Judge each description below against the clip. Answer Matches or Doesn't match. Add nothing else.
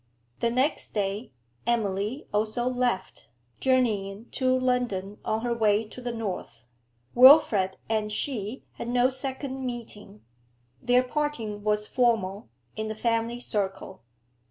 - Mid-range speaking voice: Doesn't match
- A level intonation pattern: Doesn't match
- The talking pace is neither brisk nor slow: Doesn't match